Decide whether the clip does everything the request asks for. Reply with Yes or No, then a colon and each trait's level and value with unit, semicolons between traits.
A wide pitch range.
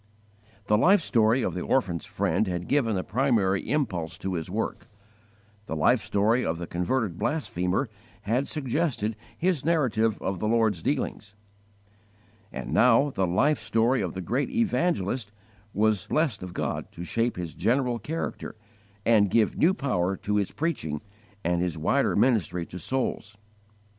Yes: wide, 6.4 semitones